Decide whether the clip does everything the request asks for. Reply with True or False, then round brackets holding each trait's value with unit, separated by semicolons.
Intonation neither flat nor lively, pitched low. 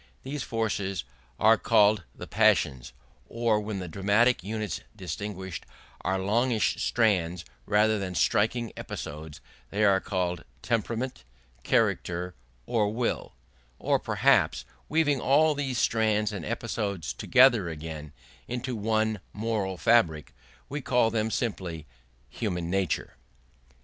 True (4.1 semitones; 105 Hz)